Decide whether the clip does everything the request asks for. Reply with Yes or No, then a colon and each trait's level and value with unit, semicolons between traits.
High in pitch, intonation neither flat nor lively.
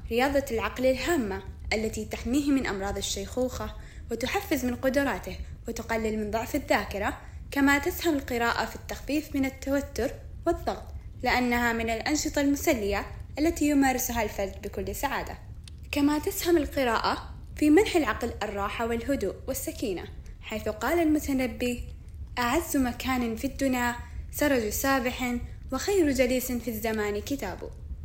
Yes: very high, 260 Hz; average, 3.9 semitones